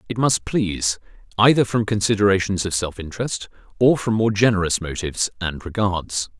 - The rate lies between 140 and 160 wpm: Yes, average, 150 wpm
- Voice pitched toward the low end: Yes, low, 100 Hz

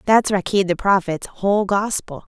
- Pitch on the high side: Yes, high, 195 Hz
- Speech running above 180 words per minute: No, average, 155 wpm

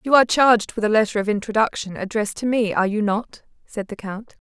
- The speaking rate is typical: No, fast, 230 wpm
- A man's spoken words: No, female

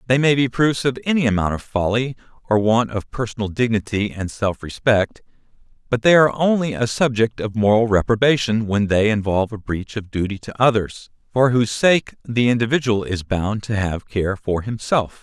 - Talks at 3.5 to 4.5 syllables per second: No, 5.2 syllables/s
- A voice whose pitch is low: Yes, low, 115 Hz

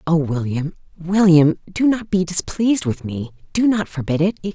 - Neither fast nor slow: Yes, average, 170 wpm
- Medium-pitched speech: Yes, medium, 175 Hz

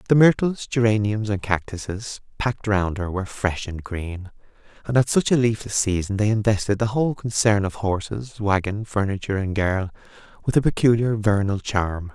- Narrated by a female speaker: No, male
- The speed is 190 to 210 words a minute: No, average, 170 wpm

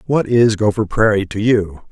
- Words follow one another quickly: No, average, 190 wpm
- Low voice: Yes, low, 105 Hz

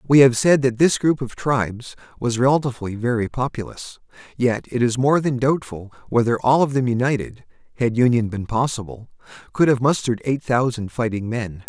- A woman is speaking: No, male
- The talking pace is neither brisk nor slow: Yes, average, 175 wpm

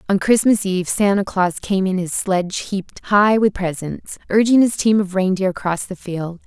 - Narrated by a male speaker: No, female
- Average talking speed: Yes, average, 195 wpm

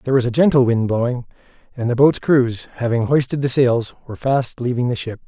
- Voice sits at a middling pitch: No, low, 125 Hz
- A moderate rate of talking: No, fast, 215 wpm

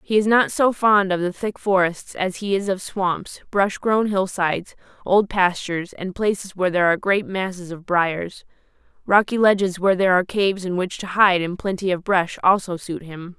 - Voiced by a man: No, female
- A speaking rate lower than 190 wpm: No, average, 200 wpm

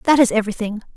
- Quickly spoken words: No, average, 190 wpm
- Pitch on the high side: Yes, high, 230 Hz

